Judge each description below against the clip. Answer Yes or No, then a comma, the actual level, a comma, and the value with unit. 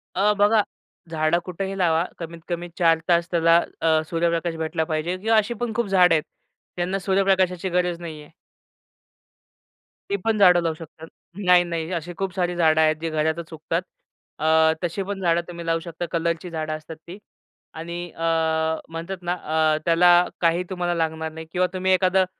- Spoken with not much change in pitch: Yes, narrow, 2.0 semitones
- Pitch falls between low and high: Yes, medium, 170 Hz